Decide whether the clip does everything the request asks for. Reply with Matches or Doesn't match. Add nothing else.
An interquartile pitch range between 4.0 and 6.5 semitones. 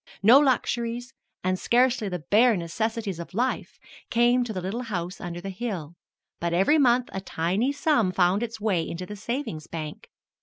Matches